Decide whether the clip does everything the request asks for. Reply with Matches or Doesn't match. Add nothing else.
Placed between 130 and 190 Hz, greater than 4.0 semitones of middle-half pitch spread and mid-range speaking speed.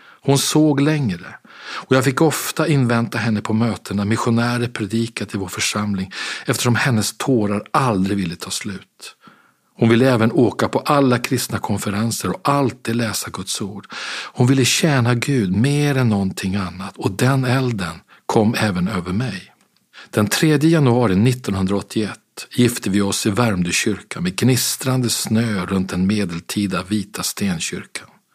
Doesn't match